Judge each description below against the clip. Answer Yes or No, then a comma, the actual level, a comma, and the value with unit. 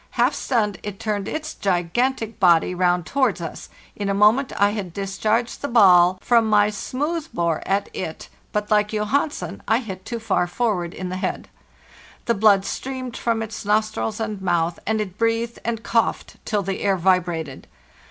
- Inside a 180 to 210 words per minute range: No, average, 170 wpm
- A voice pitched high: Yes, high, 210 Hz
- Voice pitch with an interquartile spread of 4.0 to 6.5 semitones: No, average, 3.6 semitones